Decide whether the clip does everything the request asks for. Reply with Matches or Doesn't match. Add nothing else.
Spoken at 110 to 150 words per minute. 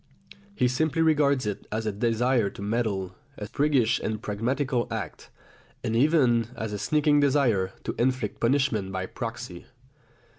Matches